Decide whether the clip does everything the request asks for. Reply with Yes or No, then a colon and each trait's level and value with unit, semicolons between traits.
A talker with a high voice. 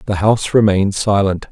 No: low, 100 Hz